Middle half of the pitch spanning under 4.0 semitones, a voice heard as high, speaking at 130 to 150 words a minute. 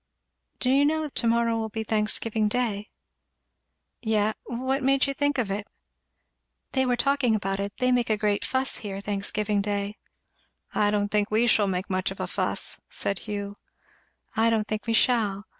No: average, 3.3 semitones; high, 220 Hz; average, 175 wpm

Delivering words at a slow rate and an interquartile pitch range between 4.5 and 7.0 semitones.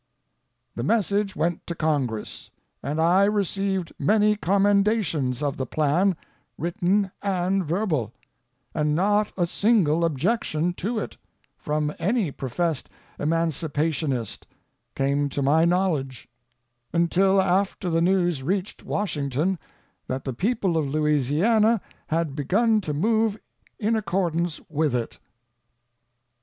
Yes: slow, 115 wpm; average, 4.9 semitones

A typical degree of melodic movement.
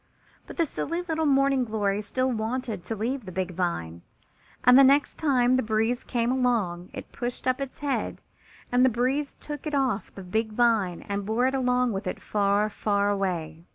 Yes: average, 4.5 semitones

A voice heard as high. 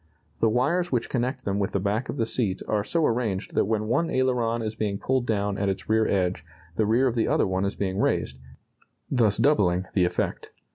No: low, 110 Hz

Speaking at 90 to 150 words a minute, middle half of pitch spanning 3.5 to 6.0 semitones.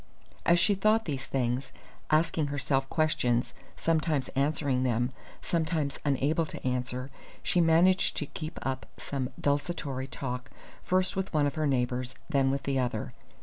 Yes: average, 145 wpm; average, 3.8 semitones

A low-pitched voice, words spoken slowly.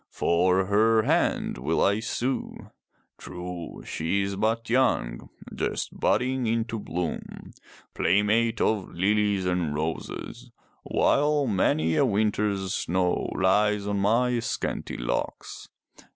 Yes: low, 100 Hz; slow, 110 wpm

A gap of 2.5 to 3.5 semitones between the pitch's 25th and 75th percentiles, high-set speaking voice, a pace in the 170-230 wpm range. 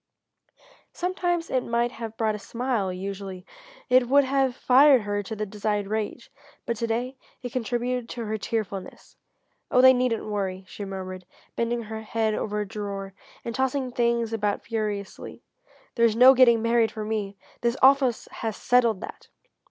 No: average, 3.1 semitones; high, 230 Hz; average, 160 wpm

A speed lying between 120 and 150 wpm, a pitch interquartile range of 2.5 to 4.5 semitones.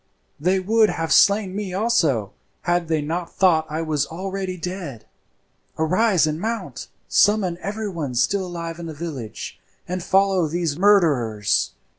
Yes: average, 140 wpm; average, 3.7 semitones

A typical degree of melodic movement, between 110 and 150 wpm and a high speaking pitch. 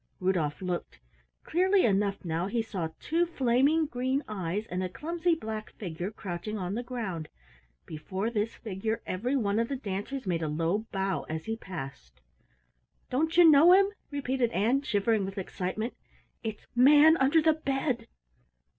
No: wide, 6.5 semitones; average, 145 wpm; high, 220 Hz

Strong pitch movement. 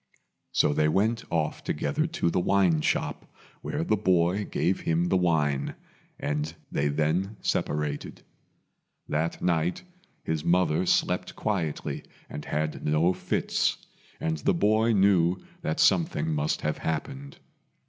No: average, 3.8 semitones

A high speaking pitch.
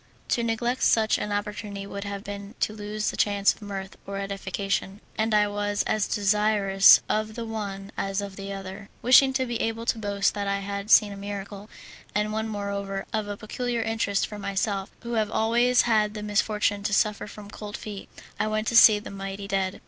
Yes: high, 205 Hz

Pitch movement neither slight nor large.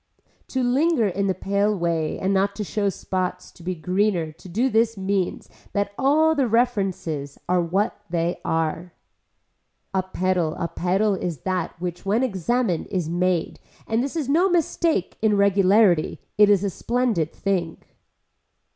Yes: average, 4.0 semitones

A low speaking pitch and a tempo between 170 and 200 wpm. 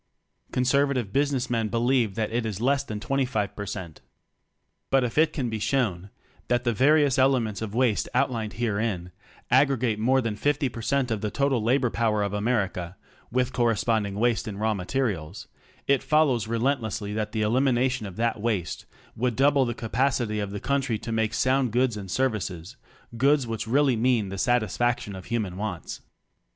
Yes: low, 115 Hz; average, 175 wpm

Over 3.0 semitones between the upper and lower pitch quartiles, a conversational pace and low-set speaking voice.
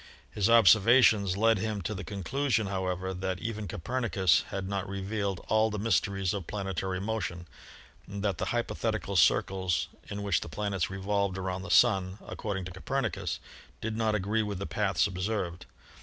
No: narrow, 2.5 semitones; average, 160 wpm; low, 100 Hz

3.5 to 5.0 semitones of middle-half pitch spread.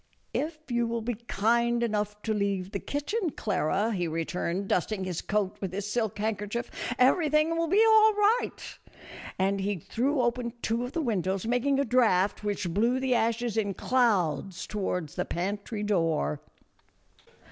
Yes: average, 4.2 semitones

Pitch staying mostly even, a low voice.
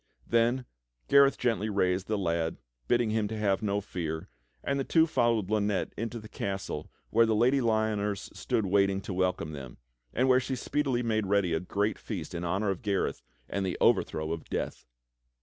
No: average, 3.8 semitones; low, 105 Hz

